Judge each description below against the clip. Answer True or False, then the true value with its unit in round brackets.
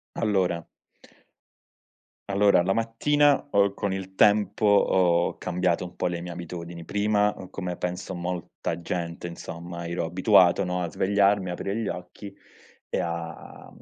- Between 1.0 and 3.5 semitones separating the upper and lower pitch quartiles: True (2.7 semitones)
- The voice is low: True (90 Hz)